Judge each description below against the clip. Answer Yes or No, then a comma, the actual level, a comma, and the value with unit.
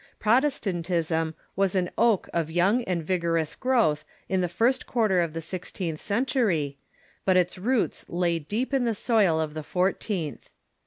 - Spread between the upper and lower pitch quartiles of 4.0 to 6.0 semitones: Yes, average, 5.0 semitones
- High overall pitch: No, medium, 180 Hz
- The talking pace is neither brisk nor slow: Yes, average, 155 wpm